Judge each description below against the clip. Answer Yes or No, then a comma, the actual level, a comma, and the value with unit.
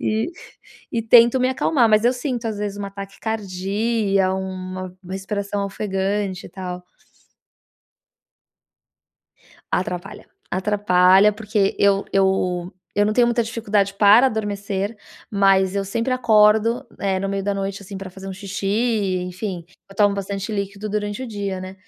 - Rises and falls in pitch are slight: Yes, narrow, 2.0 semitones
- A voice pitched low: No, high, 200 Hz